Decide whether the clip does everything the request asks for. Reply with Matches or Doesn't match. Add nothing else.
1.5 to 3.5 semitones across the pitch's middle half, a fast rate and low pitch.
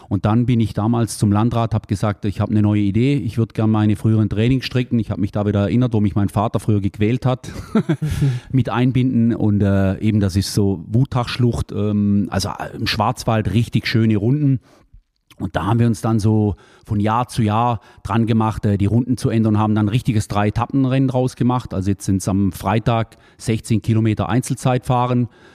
Matches